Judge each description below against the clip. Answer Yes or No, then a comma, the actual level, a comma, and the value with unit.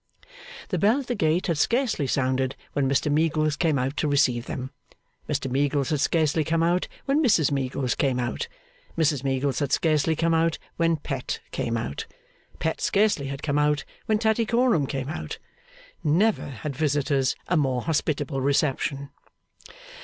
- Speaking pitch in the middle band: Yes, medium, 150 Hz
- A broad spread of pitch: No, average, 3.3 semitones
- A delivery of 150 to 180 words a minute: Yes, average, 160 wpm